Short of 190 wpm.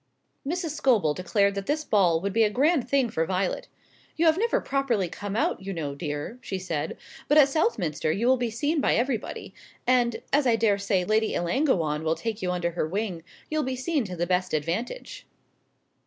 No: average, 195 wpm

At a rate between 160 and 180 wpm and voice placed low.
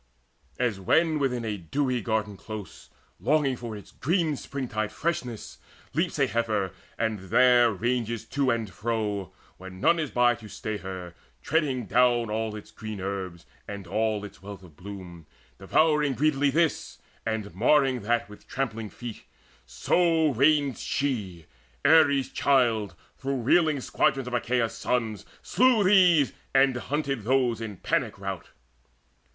No: average, 140 wpm; low, 120 Hz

